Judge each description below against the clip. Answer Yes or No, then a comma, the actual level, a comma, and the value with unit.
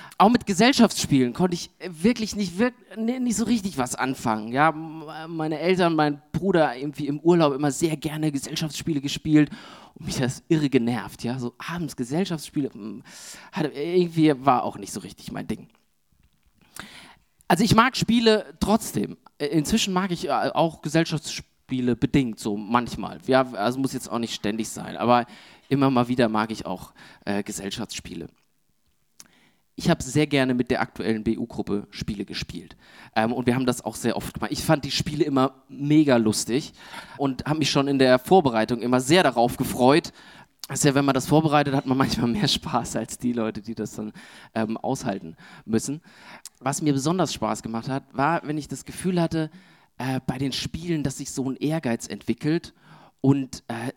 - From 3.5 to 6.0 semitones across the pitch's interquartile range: Yes, average, 5.1 semitones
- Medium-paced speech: Yes, average, 170 wpm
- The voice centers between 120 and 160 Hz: Yes, medium, 140 Hz